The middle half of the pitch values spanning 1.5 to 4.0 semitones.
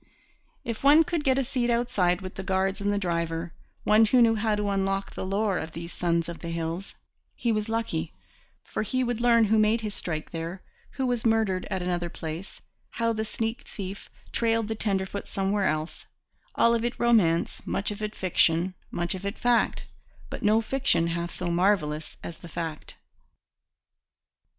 No: average, 4.7 semitones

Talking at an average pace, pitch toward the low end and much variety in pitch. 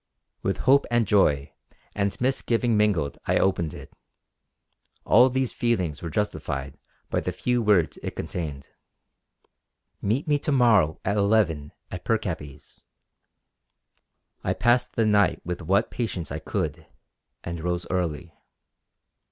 No: slow, 125 wpm; low, 100 Hz; wide, 5.9 semitones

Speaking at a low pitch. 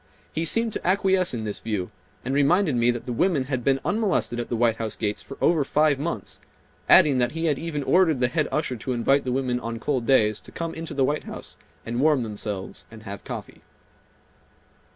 Yes: low, 130 Hz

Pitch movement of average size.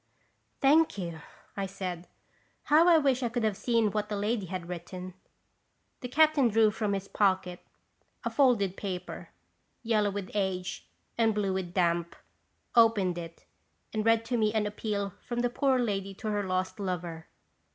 Yes: average, 3.7 semitones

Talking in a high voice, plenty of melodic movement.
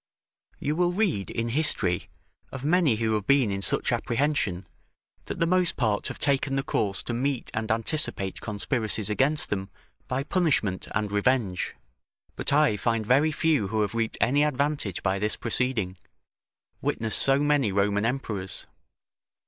No: low, 115 Hz; wide, 5.7 semitones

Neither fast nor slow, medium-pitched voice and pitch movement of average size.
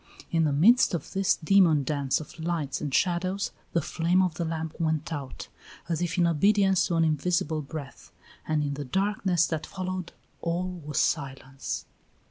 Yes: average, 170 wpm; medium, 165 Hz; average, 3.3 semitones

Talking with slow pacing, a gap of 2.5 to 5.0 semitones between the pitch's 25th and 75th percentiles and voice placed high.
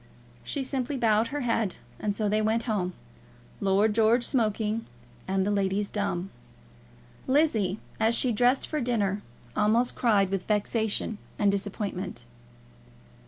Yes: slow, 130 wpm; average, 2.8 semitones; high, 215 Hz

